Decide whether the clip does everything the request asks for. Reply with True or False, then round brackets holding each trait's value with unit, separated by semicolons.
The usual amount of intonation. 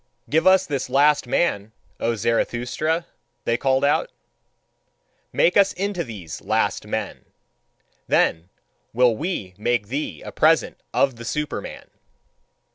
False (5.8 semitones)